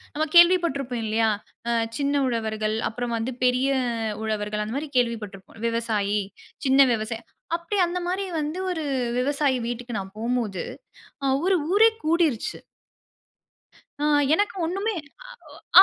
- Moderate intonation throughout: No, wide, 6.4 semitones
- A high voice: Yes, very high, 250 Hz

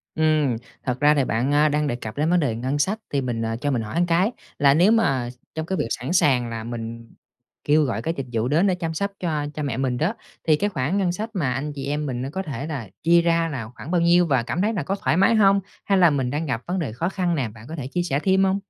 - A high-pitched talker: No, medium, 150 Hz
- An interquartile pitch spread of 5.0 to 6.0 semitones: Yes, average, 5.3 semitones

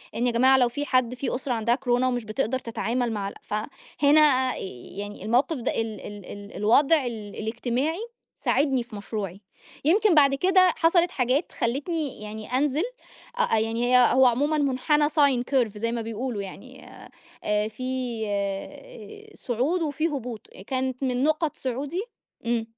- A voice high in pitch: Yes, very high, 250 Hz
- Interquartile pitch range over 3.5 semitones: Yes, average, 4.0 semitones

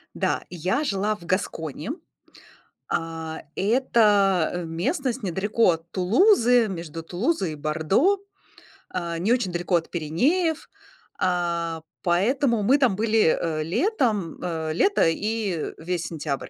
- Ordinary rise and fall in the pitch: No, wide, 5.8 semitones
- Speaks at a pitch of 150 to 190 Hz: Yes, medium, 185 Hz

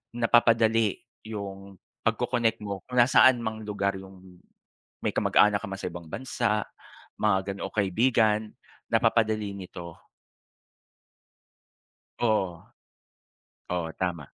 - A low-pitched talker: Yes, low, 105 Hz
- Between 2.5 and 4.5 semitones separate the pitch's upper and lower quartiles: Yes, average, 2.8 semitones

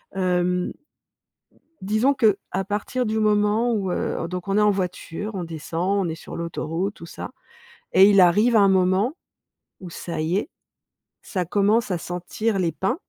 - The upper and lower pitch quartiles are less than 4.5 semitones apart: Yes, average, 3.0 semitones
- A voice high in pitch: Yes, high, 195 Hz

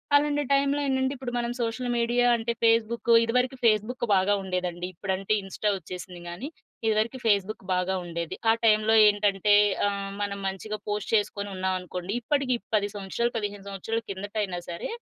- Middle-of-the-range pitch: No, high, 210 Hz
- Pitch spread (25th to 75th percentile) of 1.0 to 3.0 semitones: No, average, 3.6 semitones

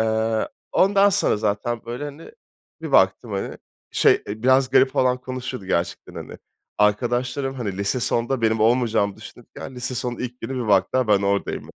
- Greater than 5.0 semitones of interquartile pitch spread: No, average, 3.5 semitones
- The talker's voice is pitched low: Yes, low, 120 Hz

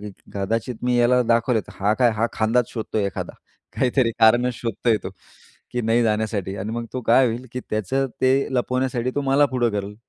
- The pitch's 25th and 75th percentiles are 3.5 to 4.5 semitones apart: No, narrow, 2.5 semitones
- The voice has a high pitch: No, low, 115 Hz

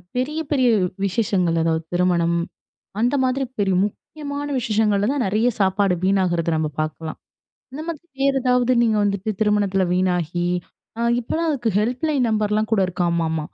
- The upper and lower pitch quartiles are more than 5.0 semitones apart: Yes, wide, 5.6 semitones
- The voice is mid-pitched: No, high, 205 Hz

